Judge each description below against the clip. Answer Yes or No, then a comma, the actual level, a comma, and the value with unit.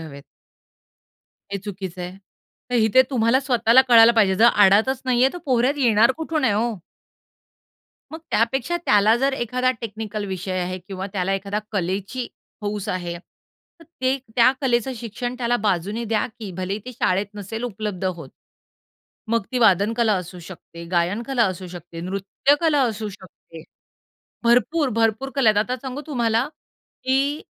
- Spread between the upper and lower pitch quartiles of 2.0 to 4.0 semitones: No, average, 4.6 semitones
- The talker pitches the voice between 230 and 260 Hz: No, high, 220 Hz